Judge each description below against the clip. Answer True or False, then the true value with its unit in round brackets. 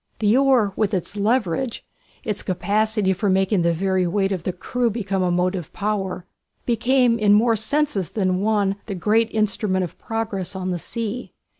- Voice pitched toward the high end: True (205 Hz)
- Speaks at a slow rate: False (170 wpm)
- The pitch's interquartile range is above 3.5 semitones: False (3.1 semitones)